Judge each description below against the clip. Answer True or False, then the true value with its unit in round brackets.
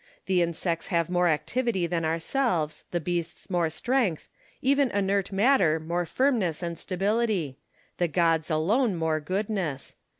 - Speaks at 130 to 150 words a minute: True (135 wpm)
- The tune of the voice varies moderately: True (4.0 semitones)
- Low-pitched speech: False (175 Hz)